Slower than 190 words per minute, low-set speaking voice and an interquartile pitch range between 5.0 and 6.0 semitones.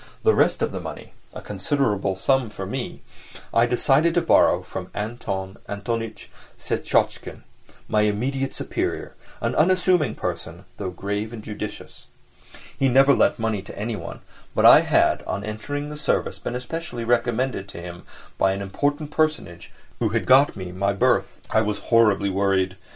Yes: average, 155 wpm; low, 110 Hz; average, 5.3 semitones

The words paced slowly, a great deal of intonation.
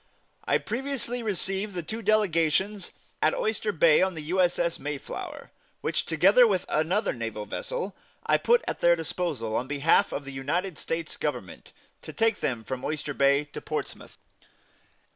No: average, 160 wpm; wide, 6.0 semitones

